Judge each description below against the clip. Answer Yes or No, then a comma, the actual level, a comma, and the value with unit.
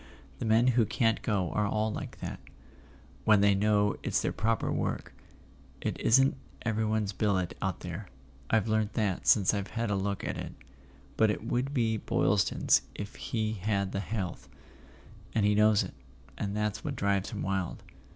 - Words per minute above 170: No, average, 165 wpm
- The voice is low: Yes, low, 105 Hz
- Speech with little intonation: Yes, narrow, 2.1 semitones